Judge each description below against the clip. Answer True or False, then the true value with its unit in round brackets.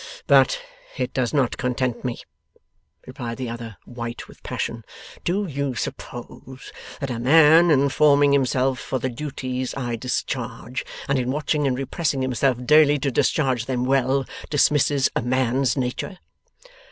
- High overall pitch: False (130 Hz)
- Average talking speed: True (145 wpm)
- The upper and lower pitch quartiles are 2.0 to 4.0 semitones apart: True (2.4 semitones)